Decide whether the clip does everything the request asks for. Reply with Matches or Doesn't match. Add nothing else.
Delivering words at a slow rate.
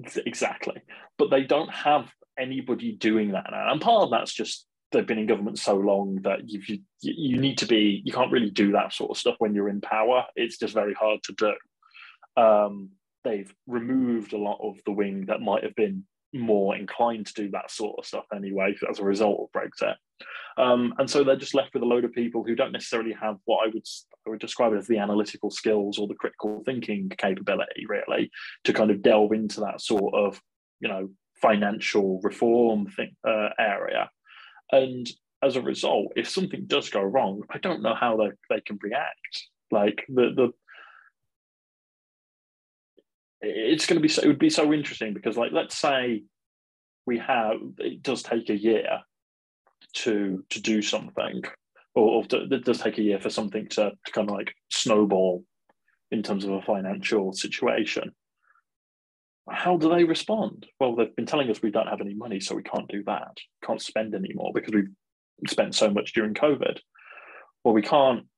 Doesn't match